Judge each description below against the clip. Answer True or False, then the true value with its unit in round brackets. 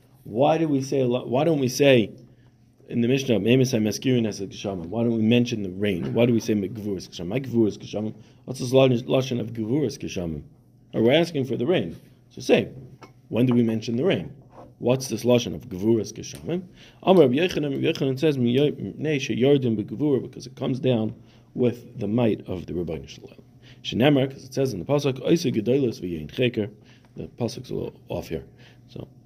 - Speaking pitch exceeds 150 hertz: False (125 Hz)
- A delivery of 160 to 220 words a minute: False (150 wpm)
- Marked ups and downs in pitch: False (2.8 semitones)